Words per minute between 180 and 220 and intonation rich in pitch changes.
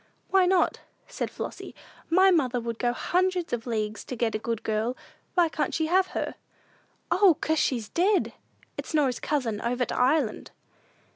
No: average, 165 wpm; wide, 7.1 semitones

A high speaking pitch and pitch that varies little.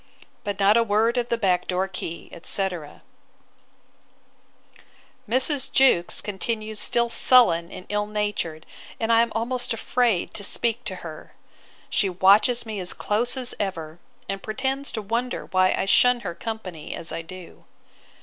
No: high, 210 Hz; average, 4.2 semitones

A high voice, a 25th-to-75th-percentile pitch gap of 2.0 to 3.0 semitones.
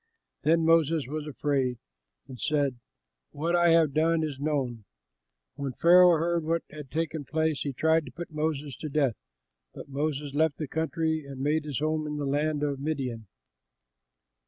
No: medium, 150 Hz; narrow, 2.4 semitones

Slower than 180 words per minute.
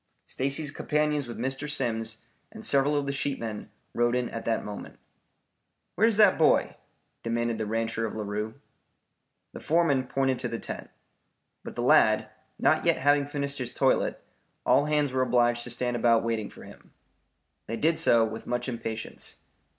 Yes: average, 165 wpm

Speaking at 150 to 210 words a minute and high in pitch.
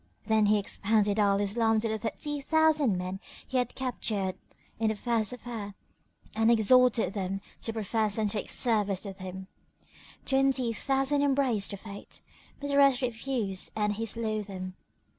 Yes: average, 160 wpm; high, 220 Hz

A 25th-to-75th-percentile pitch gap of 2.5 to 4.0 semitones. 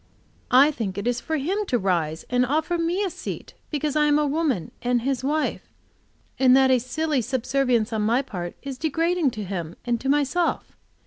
No: average, 4.6 semitones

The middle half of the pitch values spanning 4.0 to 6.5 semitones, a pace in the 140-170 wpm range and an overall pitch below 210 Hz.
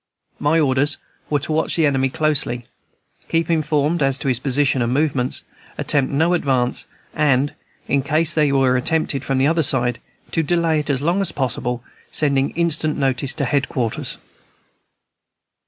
No: average, 3.0 semitones; average, 160 wpm; medium, 140 Hz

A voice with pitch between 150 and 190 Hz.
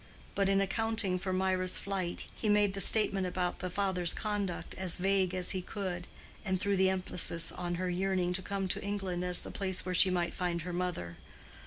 Yes: medium, 185 Hz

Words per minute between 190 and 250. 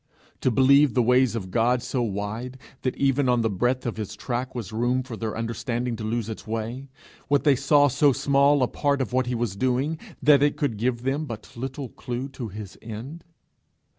Yes: fast, 205 wpm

